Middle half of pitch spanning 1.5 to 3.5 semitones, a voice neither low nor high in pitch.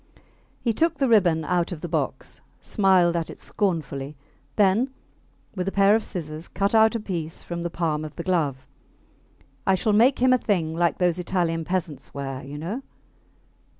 No: average, 4.2 semitones; medium, 175 Hz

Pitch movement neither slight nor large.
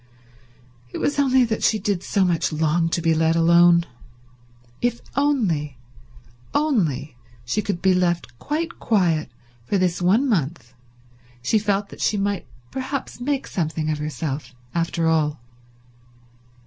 No: wide, 5.7 semitones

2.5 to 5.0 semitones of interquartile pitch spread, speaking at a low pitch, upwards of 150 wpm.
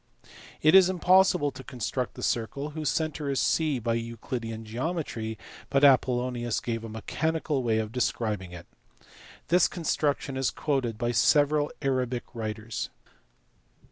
No: average, 4.5 semitones; low, 125 Hz; slow, 135 wpm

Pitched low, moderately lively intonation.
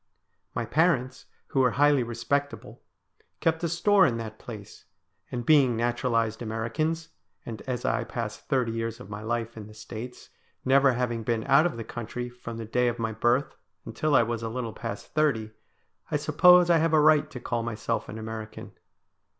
Yes: low, 120 Hz; average, 3.8 semitones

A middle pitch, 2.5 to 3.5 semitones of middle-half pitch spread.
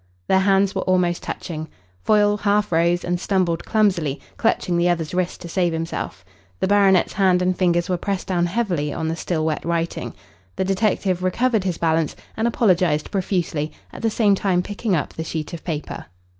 Yes: medium, 180 Hz; average, 2.9 semitones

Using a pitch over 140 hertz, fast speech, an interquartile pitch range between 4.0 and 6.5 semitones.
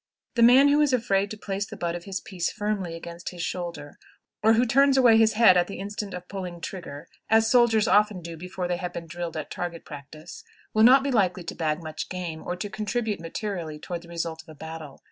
Yes: medium, 185 Hz; fast, 230 wpm; average, 4.3 semitones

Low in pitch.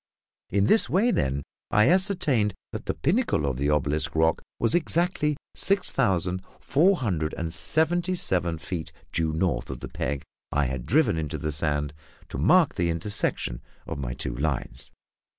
Yes: very low, 85 Hz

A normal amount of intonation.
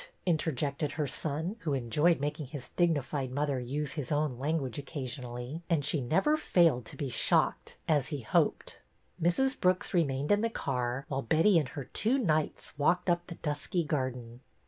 Yes: average, 4.2 semitones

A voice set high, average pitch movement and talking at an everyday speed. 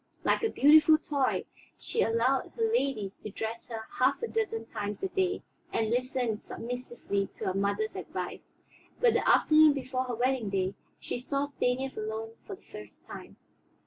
Yes: very high, 250 Hz; average, 4.7 semitones; average, 170 wpm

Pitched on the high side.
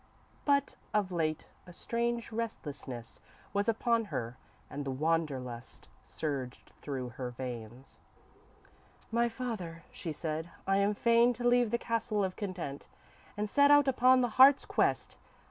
Yes: high, 195 Hz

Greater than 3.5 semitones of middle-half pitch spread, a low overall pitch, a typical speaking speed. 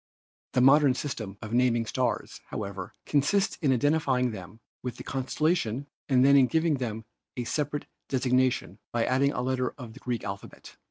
No: average, 3.1 semitones; low, 130 Hz; average, 170 wpm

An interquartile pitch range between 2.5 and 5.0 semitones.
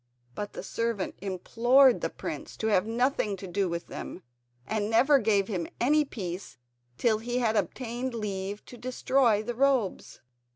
Yes: average, 3.8 semitones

